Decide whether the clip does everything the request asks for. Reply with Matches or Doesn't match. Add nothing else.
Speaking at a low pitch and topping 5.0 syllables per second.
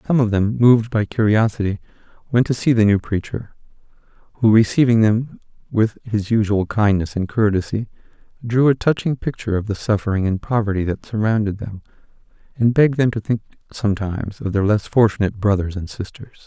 Matches